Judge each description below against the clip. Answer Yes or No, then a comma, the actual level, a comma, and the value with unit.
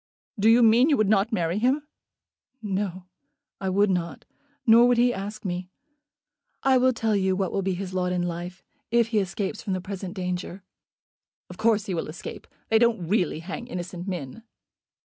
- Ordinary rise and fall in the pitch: Yes, average, 3.7 semitones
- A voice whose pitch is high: Yes, high, 195 Hz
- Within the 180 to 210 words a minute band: Yes, average, 185 wpm